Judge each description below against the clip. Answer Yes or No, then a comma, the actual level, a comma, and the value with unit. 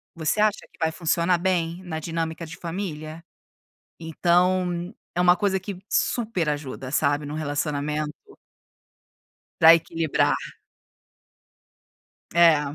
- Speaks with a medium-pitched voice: Yes, medium, 165 Hz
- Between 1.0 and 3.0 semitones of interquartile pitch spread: Yes, narrow, 2.5 semitones